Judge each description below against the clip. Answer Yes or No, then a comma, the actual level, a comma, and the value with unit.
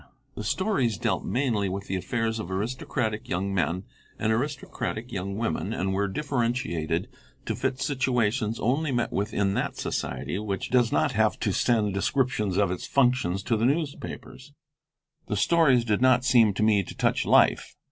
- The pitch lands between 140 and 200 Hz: No, low, 110 Hz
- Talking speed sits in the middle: Yes, average, 165 wpm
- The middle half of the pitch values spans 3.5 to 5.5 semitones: Yes, average, 4.4 semitones